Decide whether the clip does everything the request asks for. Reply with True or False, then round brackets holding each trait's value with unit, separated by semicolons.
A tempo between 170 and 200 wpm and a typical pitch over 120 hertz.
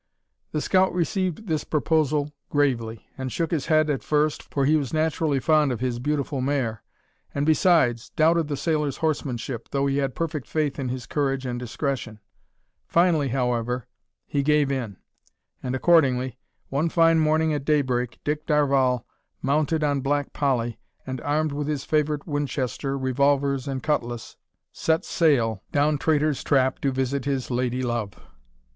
False (155 wpm; 140 Hz)